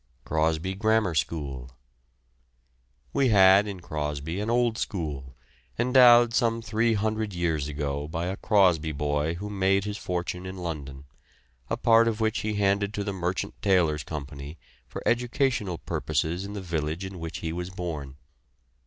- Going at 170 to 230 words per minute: No, average, 155 wpm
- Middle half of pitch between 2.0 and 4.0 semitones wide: No, average, 5.2 semitones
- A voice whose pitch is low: Yes, very low, 90 Hz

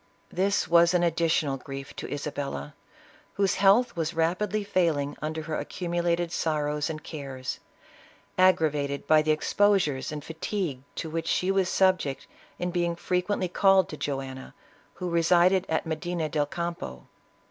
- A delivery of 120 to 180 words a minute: Yes, average, 140 wpm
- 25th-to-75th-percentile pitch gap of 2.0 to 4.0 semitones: Yes, average, 3.4 semitones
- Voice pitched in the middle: Yes, medium, 165 Hz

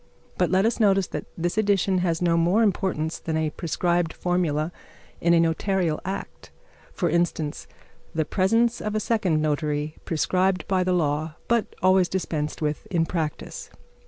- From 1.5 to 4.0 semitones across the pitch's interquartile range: Yes, average, 3.2 semitones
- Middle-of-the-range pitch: Yes, medium, 175 Hz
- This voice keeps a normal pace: Yes, average, 160 wpm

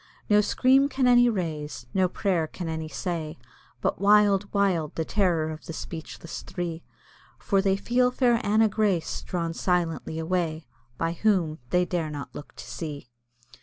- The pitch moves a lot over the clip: No, average, 4.3 semitones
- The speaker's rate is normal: Yes, average, 160 wpm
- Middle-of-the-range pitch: Yes, medium, 180 Hz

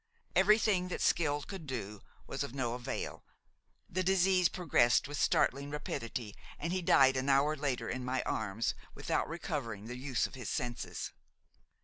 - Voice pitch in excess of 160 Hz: No, medium, 140 Hz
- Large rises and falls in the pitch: Yes, wide, 5.9 semitones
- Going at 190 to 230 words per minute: No, average, 155 wpm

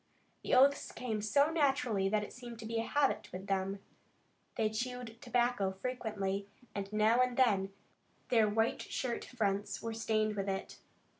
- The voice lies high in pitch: Yes, high, 220 Hz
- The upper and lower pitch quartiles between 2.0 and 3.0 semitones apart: No, average, 3.7 semitones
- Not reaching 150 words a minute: No, average, 160 wpm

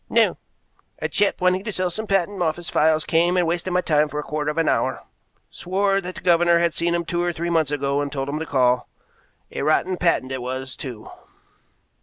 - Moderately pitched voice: Yes, medium, 170 Hz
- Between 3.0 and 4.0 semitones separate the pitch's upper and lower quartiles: Yes, average, 3.4 semitones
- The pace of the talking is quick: Yes, fast, 220 wpm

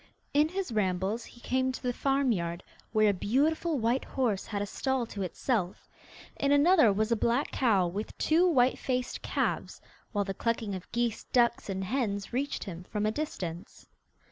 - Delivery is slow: No, average, 175 wpm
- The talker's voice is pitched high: Yes, high, 230 Hz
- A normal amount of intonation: Yes, average, 4.8 semitones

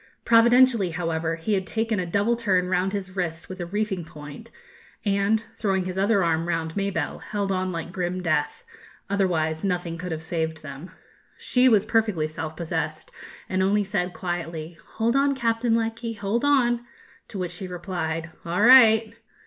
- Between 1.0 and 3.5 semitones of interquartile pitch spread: No, average, 4.6 semitones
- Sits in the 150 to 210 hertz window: Yes, medium, 185 Hz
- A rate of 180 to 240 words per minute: No, average, 165 wpm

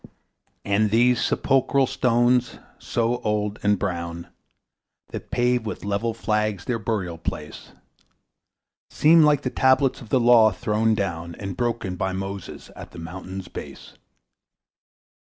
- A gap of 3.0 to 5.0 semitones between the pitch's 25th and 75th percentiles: Yes, average, 4.3 semitones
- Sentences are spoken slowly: Yes, slow, 130 wpm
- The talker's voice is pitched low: Yes, low, 110 Hz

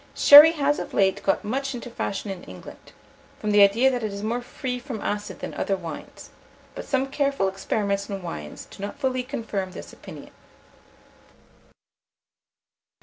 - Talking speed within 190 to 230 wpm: No, average, 160 wpm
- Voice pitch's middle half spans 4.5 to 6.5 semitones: Yes, average, 5.1 semitones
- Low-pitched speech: No, high, 220 Hz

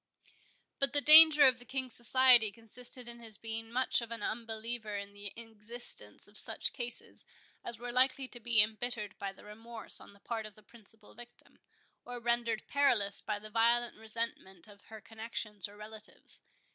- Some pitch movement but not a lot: No, narrow, 2.2 semitones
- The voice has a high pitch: Yes, high, 230 Hz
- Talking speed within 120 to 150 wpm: No, average, 170 wpm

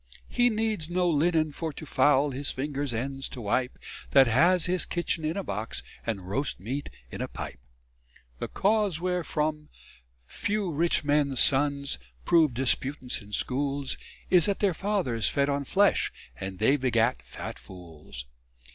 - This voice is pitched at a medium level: Yes, medium, 145 Hz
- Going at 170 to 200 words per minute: No, average, 155 wpm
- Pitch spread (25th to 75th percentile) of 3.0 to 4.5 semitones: No, average, 5.2 semitones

